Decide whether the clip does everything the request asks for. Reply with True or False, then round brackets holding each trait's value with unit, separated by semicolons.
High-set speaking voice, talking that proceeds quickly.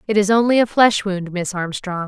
True (200 Hz; 230 wpm)